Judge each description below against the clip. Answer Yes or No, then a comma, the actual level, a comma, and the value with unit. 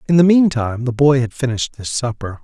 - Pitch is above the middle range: No, low, 130 Hz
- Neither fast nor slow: No, fast, 220 wpm